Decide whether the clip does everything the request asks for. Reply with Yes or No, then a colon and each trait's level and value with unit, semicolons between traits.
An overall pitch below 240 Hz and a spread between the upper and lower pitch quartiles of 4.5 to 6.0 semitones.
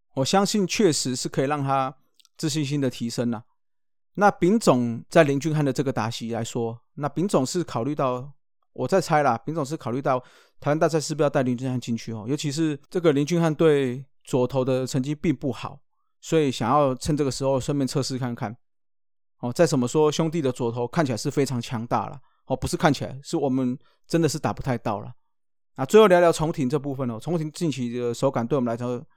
No: low, 135 Hz; average, 3.9 semitones